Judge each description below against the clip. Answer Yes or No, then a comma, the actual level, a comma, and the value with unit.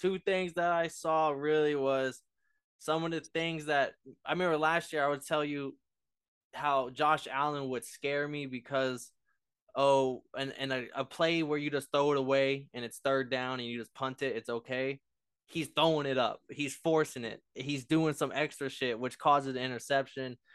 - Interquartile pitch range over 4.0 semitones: No, average, 2.8 semitones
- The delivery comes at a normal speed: Yes, average, 195 wpm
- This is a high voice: No, medium, 140 Hz